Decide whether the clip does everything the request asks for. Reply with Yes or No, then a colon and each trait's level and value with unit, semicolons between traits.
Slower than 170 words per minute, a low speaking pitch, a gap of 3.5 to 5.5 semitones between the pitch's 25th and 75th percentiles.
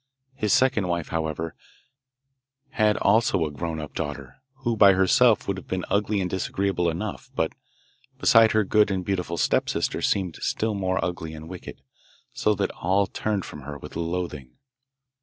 Yes: average, 160 wpm; very low, 95 Hz; average, 4.2 semitones